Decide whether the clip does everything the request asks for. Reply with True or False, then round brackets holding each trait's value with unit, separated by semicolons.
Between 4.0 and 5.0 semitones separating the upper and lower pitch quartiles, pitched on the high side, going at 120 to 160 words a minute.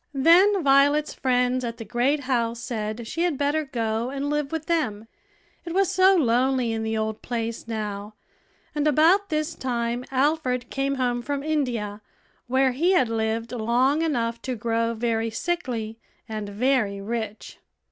True (4.3 semitones; 250 Hz; 155 wpm)